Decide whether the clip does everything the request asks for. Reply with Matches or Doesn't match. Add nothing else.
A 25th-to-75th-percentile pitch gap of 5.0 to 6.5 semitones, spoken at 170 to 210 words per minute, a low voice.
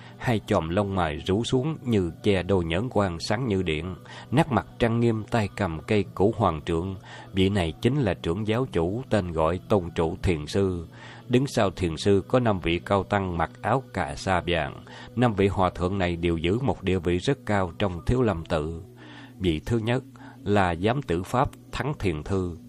Matches